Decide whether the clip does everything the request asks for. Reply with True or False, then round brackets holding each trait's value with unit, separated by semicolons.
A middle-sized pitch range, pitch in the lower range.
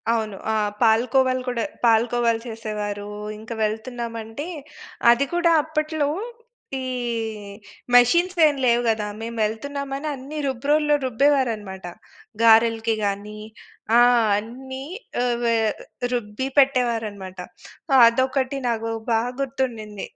False (3.3 semitones; 235 Hz)